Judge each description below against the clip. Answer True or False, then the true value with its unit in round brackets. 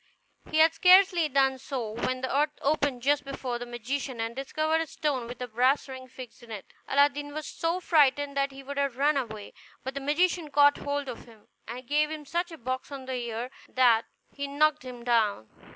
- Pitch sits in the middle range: False (275 Hz)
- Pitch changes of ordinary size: True (3.0 semitones)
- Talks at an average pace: False (210 wpm)